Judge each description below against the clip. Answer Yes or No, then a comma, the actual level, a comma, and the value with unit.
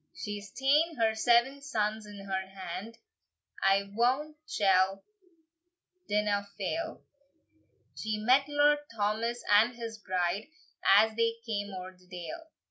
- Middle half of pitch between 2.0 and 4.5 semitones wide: Yes, average, 3.4 semitones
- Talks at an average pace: No, slow, 125 wpm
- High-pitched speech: Yes, high, 215 Hz